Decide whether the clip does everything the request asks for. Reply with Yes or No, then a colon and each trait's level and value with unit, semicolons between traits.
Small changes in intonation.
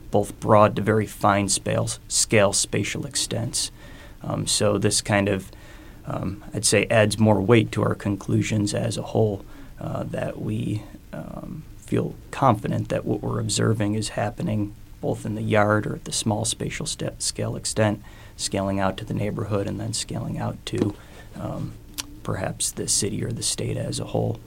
Yes: narrow, 1.4 semitones